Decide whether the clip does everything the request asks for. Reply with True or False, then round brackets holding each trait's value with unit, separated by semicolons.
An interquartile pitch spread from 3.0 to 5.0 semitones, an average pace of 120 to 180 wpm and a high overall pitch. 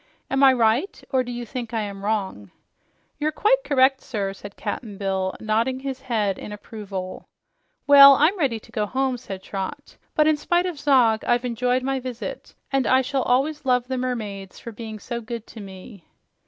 False (4.2 semitones; 190 wpm; 245 Hz)